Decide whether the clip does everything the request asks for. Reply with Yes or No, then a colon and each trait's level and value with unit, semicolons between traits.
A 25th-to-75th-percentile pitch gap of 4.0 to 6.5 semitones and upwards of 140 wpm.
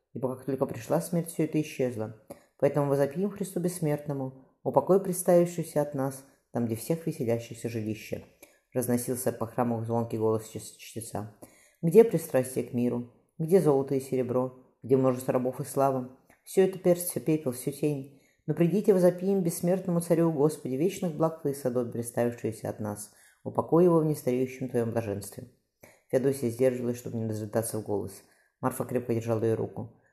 Yes: average, 5.2 semitones; average, 155 wpm